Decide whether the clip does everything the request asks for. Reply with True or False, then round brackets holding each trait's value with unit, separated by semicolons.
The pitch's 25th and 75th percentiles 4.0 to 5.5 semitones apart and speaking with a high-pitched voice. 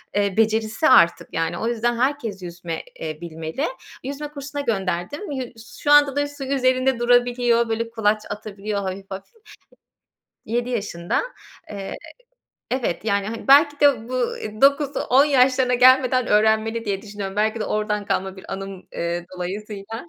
True (4.7 semitones; 225 Hz)